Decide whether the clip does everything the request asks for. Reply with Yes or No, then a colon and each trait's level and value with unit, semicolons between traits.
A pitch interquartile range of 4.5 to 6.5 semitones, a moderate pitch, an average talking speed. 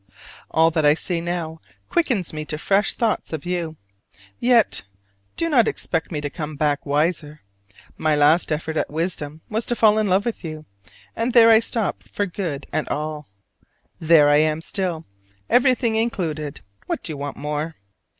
Yes: wide, 5.4 semitones; medium, 165 Hz; average, 170 wpm